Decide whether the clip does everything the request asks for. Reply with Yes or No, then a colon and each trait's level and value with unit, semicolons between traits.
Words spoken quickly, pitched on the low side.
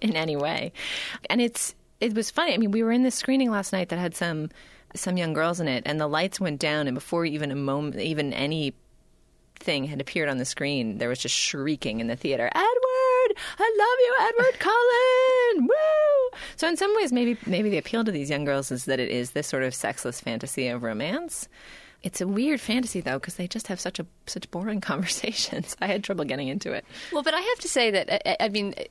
No: fast, 230 wpm; high, 190 Hz